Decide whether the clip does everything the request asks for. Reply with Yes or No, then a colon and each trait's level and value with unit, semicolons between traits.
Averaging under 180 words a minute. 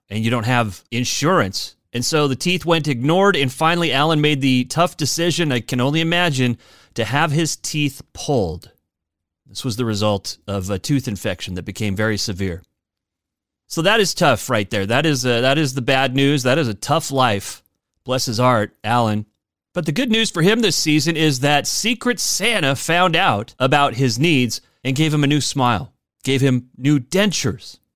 No: average, 190 wpm